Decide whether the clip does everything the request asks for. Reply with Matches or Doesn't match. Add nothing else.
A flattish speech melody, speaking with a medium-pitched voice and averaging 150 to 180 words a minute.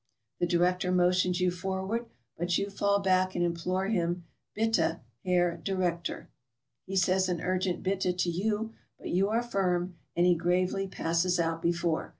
Matches